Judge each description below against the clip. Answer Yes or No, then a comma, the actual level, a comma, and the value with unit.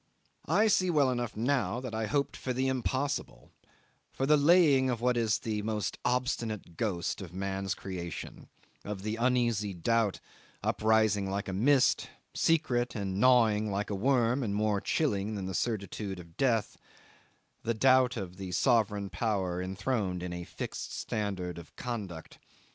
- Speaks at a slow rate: No, average, 155 wpm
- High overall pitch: No, low, 110 Hz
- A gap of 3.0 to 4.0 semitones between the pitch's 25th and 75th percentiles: No, average, 4.4 semitones